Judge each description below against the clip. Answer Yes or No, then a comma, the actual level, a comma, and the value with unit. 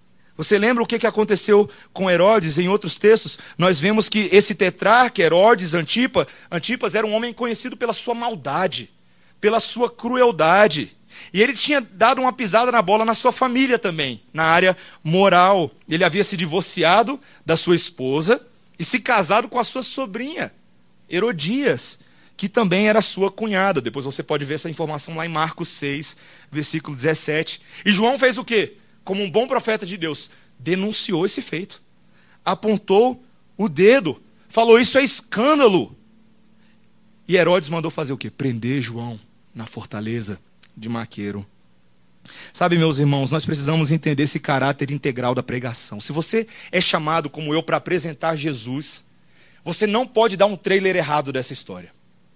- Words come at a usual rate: Yes, average, 155 wpm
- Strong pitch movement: Yes, wide, 6.5 semitones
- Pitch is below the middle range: No, medium, 180 Hz